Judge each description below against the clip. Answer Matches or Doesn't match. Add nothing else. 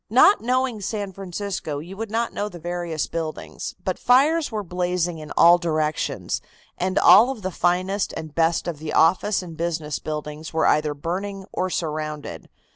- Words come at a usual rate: Matches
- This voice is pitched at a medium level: Matches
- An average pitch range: Matches